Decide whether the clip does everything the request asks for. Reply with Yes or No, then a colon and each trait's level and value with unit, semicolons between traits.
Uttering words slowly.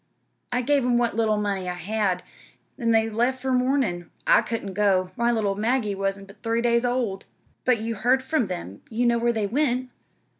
No: average, 195 wpm